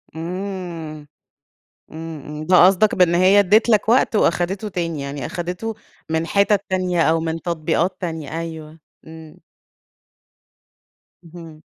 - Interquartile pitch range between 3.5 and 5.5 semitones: No, narrow, 2.6 semitones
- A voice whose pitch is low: No, medium, 170 Hz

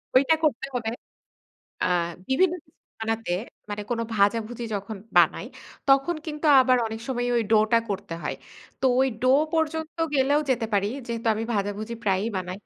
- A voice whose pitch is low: No, high, 235 Hz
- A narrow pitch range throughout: No, average, 4.2 semitones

